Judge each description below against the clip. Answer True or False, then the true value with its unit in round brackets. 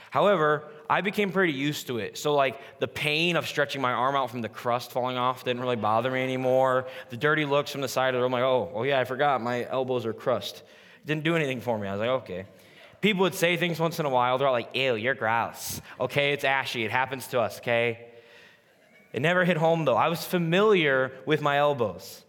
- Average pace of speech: False (235 wpm)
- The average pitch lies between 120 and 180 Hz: True (135 Hz)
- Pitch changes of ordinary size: True (3.5 semitones)